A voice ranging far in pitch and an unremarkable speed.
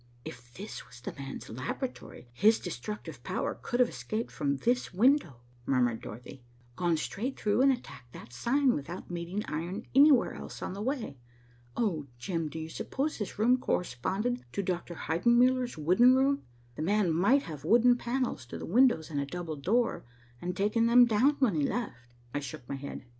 Yes: wide, 8.7 semitones; average, 180 wpm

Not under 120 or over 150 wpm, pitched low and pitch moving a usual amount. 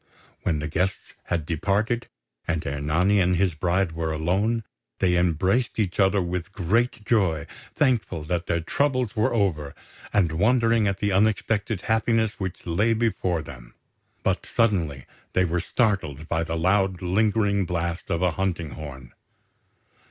Yes: average, 145 wpm; very low, 95 Hz; average, 4.3 semitones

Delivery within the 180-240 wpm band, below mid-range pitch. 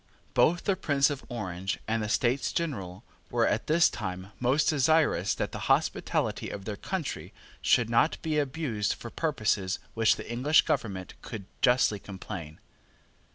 No: average, 155 wpm; low, 120 Hz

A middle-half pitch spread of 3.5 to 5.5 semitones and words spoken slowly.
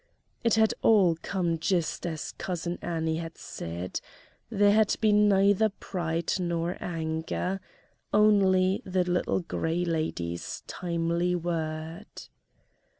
No: average, 2.9 semitones; slow, 110 wpm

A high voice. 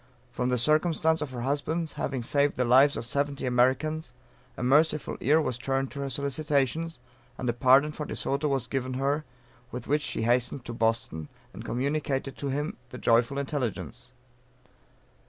No: low, 135 Hz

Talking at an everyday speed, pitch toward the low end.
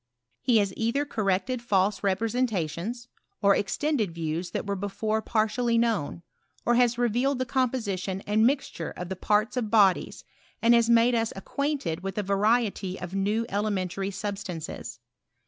No: average, 165 wpm; high, 210 Hz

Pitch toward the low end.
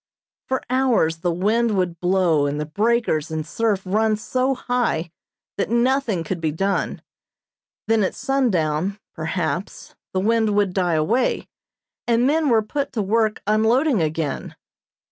No: high, 205 Hz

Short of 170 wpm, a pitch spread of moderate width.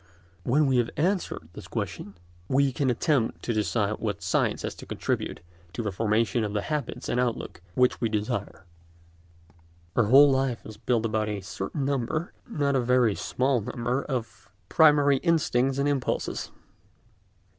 Yes: average, 150 wpm; average, 4.3 semitones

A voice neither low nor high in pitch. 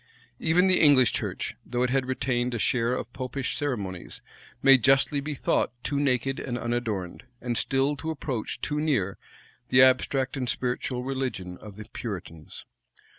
No: low, 125 Hz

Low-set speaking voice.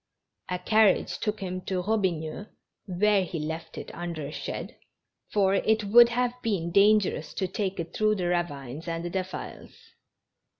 No: medium, 185 Hz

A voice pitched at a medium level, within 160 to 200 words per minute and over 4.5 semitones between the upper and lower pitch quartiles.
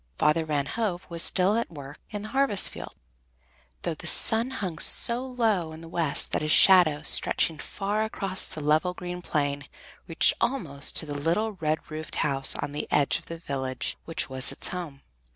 Yes: medium, 165 Hz; average, 190 wpm; average, 5.0 semitones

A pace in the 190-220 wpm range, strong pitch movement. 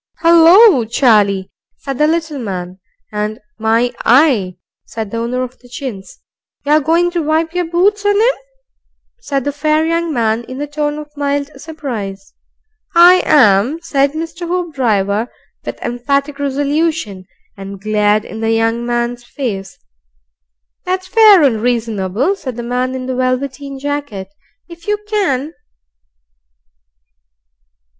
No: slow, 135 wpm; wide, 6.1 semitones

